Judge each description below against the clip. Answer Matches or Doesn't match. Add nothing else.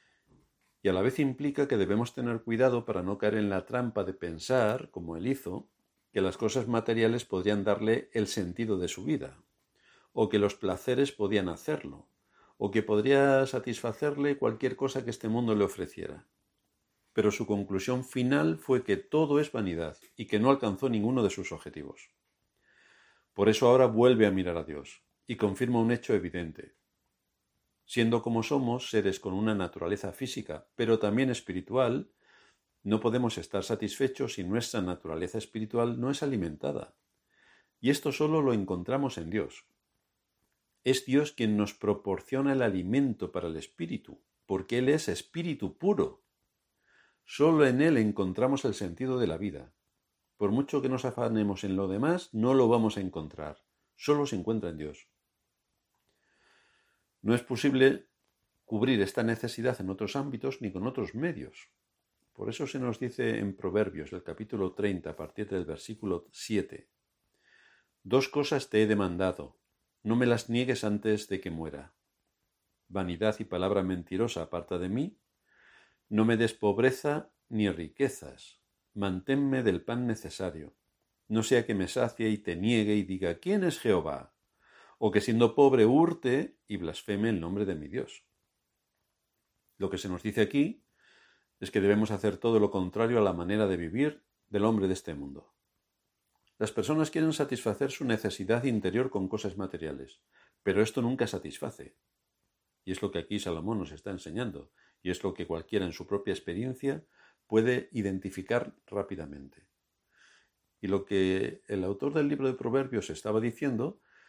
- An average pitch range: Matches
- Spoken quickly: Doesn't match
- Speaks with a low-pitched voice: Matches